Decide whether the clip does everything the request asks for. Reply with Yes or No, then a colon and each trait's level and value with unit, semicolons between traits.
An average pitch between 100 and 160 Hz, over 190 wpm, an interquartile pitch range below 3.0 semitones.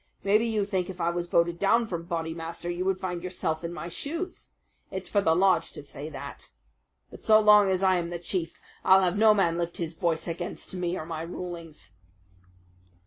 No: medium, 175 Hz; average, 200 wpm; narrow, 2.4 semitones